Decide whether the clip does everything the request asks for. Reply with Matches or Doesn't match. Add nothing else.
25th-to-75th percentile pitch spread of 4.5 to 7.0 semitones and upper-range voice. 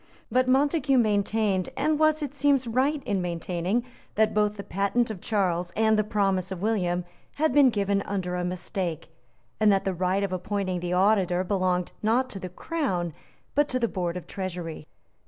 Matches